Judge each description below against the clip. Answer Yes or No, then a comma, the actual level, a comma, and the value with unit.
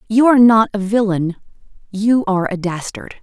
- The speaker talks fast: No, average, 165 wpm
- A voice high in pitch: Yes, high, 205 Hz